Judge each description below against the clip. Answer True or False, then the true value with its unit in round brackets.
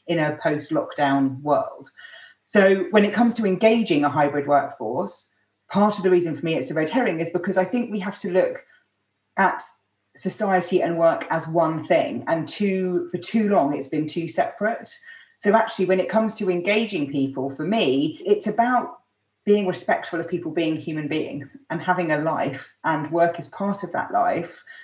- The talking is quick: False (185 wpm)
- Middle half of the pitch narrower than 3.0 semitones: False (4.9 semitones)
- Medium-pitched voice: True (180 Hz)